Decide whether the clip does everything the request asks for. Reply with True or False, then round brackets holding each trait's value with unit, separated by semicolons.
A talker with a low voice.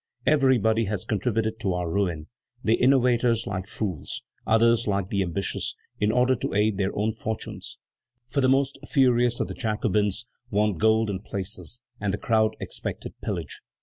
True (110 Hz)